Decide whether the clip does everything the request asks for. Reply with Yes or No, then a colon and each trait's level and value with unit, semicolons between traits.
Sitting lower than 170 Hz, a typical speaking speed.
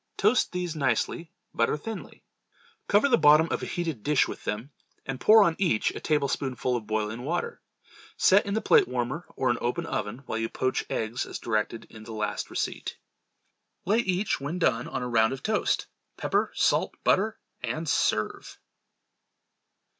Yes: medium, 140 Hz; average, 170 wpm